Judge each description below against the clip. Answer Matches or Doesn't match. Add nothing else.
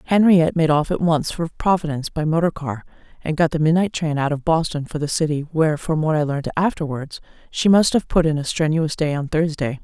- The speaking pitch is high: Doesn't match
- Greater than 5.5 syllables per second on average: Matches